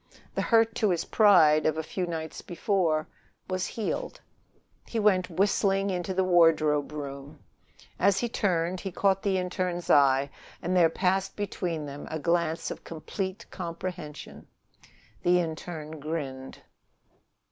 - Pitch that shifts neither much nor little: Yes, average, 3.4 semitones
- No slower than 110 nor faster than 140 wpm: Yes, slow, 135 wpm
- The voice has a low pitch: No, medium, 175 Hz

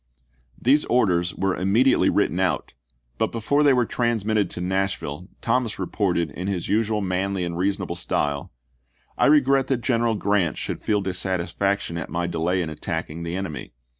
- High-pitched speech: No, very low, 95 Hz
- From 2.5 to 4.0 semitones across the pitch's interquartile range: No, average, 4.7 semitones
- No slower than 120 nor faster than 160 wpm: No, average, 170 wpm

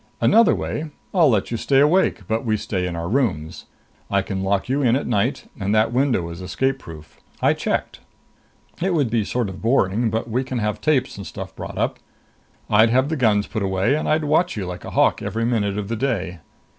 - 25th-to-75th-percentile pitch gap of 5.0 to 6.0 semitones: Yes, wide, 5.4 semitones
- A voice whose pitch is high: No, low, 115 Hz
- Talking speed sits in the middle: No, fast, 220 wpm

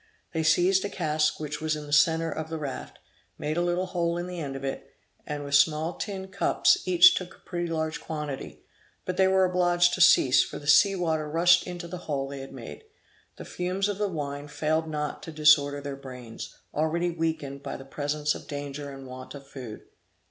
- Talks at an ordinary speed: No, fast, 210 wpm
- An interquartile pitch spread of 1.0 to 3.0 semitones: No, average, 3.5 semitones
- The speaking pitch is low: No, medium, 155 Hz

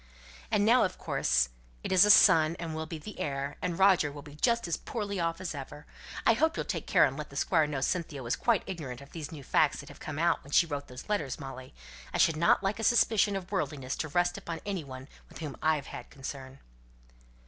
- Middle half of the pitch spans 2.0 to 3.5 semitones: No, average, 5.1 semitones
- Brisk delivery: Yes, fast, 240 wpm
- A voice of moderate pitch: Yes, medium, 160 Hz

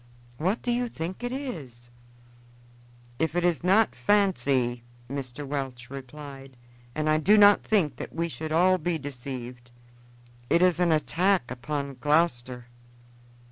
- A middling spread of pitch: No, wide, 5.7 semitones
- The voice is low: No, medium, 155 Hz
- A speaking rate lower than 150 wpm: Yes, average, 140 wpm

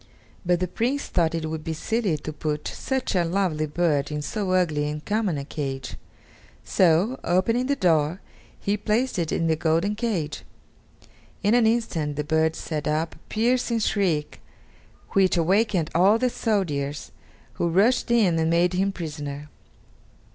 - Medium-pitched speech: Yes, medium, 175 Hz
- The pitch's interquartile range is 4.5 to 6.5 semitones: Yes, average, 5.3 semitones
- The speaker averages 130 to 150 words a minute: No, average, 160 wpm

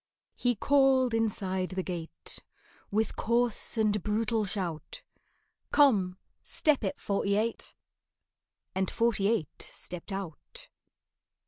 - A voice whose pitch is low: No, high, 210 Hz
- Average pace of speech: No, slow, 105 wpm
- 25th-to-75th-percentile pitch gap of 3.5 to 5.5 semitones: Yes, average, 3.8 semitones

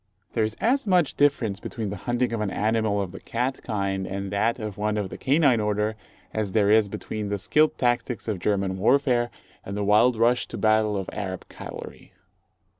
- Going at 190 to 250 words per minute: Yes, average, 195 wpm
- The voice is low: Yes, low, 110 Hz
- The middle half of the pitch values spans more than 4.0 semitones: No, average, 3.2 semitones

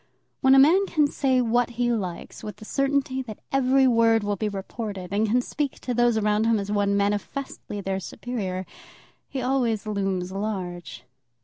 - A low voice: No, high, 220 Hz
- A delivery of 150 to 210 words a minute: Yes, average, 175 wpm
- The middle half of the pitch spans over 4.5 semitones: No, average, 4.1 semitones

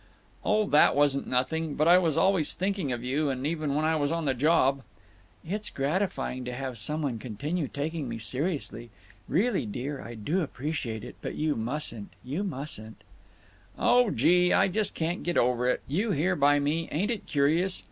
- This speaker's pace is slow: No, average, 170 wpm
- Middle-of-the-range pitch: Yes, medium, 150 Hz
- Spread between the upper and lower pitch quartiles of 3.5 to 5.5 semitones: Yes, average, 5.1 semitones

